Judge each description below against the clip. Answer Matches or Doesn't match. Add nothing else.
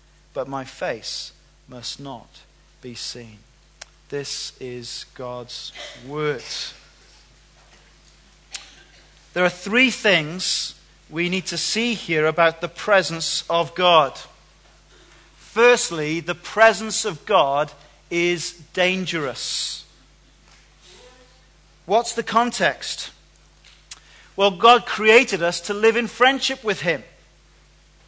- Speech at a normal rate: Doesn't match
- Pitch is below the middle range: Doesn't match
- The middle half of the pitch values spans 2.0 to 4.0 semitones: Doesn't match